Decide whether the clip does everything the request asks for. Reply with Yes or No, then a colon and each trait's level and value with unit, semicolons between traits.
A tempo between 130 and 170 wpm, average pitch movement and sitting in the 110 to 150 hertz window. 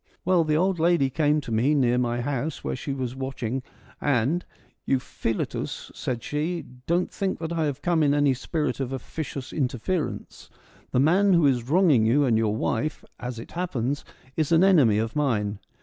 No: average, 185 wpm; average, 4.6 semitones; medium, 140 Hz